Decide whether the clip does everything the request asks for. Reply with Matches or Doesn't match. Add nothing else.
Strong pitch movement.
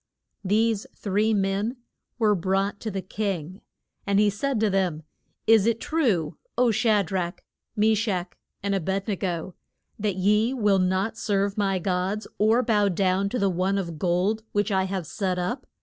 Doesn't match